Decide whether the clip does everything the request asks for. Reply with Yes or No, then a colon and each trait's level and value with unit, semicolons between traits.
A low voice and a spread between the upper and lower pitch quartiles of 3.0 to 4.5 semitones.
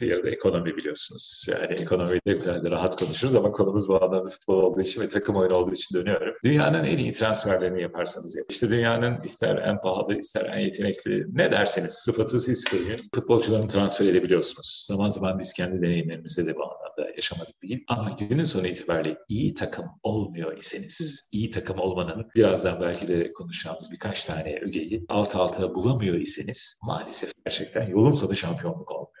Yes: very low, 95 Hz; average, 3.9 semitones